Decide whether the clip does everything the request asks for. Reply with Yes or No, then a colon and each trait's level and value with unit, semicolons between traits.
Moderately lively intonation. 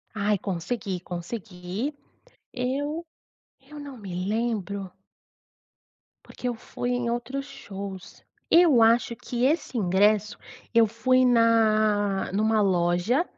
Yes: average, 4.0 semitones